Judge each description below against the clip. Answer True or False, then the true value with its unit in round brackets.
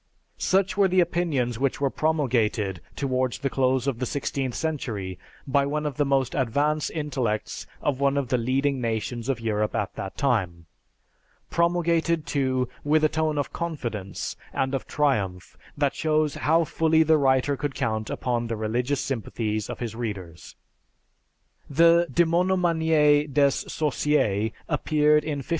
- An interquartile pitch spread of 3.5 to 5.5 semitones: True (4.5 semitones)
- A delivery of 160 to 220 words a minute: False (150 wpm)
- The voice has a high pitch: False (140 Hz)